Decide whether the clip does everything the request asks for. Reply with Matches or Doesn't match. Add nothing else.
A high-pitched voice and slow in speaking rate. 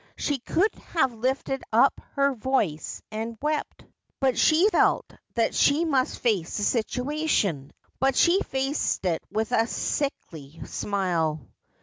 Matches